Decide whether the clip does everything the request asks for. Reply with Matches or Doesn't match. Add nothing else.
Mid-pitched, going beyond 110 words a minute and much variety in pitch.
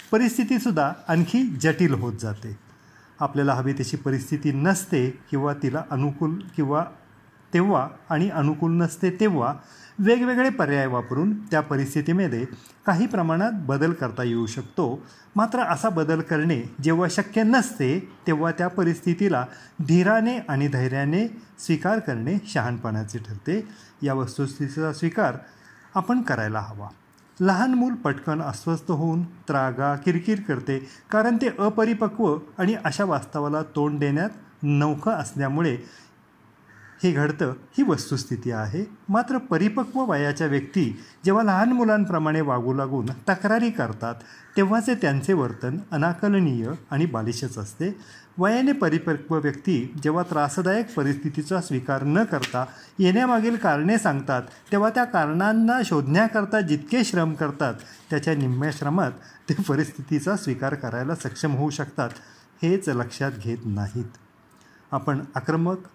Matches